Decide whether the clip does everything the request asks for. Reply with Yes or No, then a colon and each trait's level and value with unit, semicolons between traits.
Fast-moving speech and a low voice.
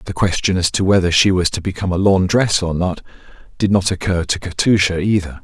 Yes: fast, 210 wpm; very low, 90 Hz